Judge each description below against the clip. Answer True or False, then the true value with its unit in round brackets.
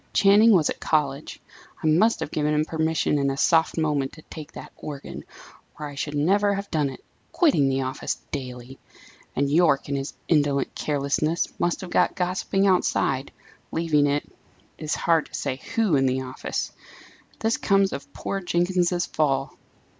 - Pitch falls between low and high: True (155 Hz)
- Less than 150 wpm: False (170 wpm)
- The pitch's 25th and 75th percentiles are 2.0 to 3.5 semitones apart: False (4.1 semitones)